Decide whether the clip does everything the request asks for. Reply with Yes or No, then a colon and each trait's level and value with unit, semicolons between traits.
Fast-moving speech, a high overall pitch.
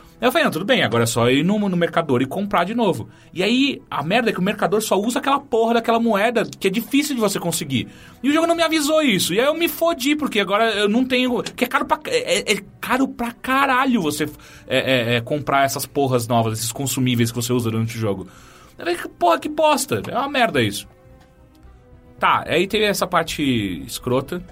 Yes: fast, 220 wpm; high, 200 Hz